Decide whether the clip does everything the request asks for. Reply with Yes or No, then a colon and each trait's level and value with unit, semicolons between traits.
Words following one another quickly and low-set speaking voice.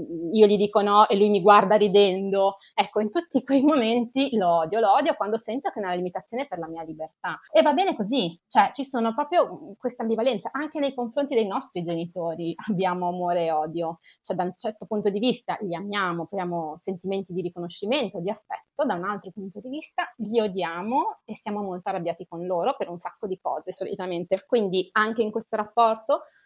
No: fast, 200 wpm; high, 210 Hz